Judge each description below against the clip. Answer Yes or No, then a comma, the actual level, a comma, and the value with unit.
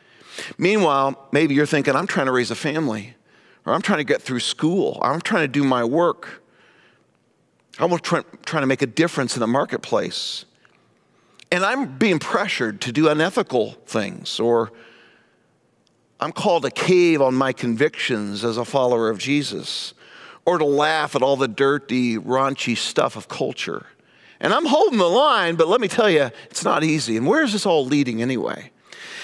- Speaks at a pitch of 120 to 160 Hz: Yes, medium, 140 Hz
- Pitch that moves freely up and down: No, average, 4.5 semitones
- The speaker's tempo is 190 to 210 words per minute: No, average, 175 wpm